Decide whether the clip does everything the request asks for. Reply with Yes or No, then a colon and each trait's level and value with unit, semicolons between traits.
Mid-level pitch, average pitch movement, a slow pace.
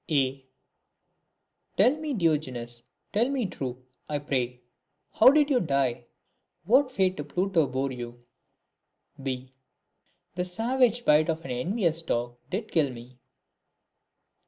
No: medium, 155 Hz; wide, 8.5 semitones; slow, 125 wpm